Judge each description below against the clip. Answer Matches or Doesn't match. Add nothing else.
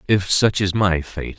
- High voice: Doesn't match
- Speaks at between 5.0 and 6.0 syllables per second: Doesn't match